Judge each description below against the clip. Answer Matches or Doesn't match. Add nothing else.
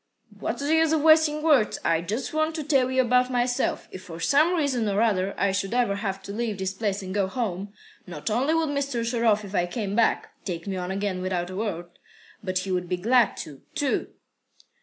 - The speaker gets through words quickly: Matches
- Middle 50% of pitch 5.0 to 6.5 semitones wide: Matches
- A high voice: Matches